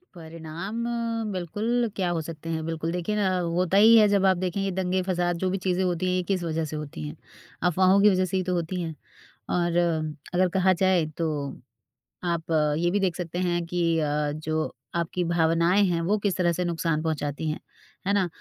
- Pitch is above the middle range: No, medium, 175 Hz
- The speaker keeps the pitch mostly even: Yes, narrow, 2.3 semitones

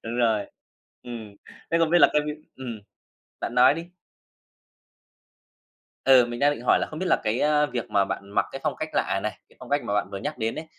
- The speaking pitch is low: Yes, low, 125 Hz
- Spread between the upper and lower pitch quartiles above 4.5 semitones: Yes, average, 5.0 semitones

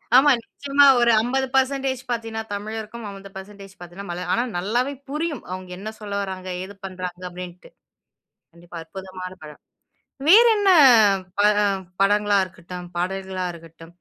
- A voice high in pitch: Yes, high, 200 Hz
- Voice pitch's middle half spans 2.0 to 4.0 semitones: No, average, 4.7 semitones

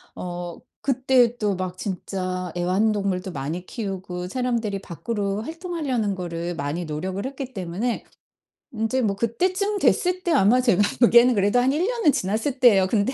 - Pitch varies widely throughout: Yes, wide, 5.7 semitones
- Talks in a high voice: Yes, high, 210 Hz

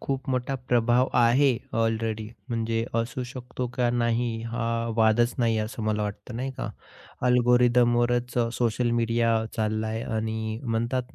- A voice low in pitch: Yes, low, 120 Hz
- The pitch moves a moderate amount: No, narrow, 1.6 semitones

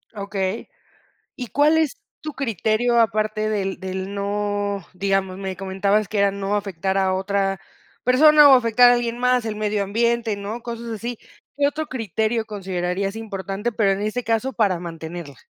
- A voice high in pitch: Yes, high, 210 Hz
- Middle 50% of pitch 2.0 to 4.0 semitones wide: Yes, average, 3.3 semitones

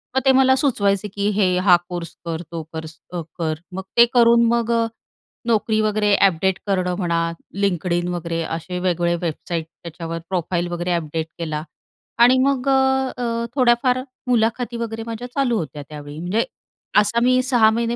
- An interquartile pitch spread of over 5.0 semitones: Yes, wide, 5.5 semitones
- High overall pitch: Yes, high, 200 Hz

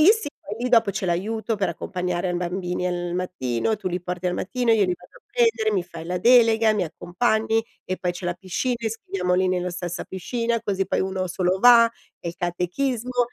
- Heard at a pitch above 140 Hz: Yes, high, 190 Hz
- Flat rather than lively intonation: No, average, 4.1 semitones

